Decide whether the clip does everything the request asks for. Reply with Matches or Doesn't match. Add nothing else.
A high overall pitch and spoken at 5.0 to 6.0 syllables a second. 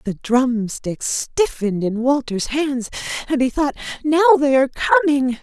Doesn't match